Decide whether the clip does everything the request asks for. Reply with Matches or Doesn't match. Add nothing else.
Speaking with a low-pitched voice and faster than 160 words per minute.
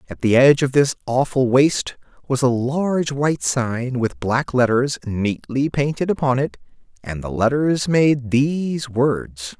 Doesn't match